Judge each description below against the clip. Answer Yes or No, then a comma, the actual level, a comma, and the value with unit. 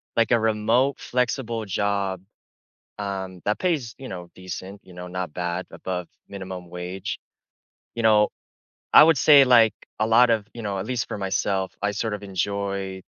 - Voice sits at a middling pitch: No, low, 100 Hz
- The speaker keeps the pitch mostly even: No, average, 3.6 semitones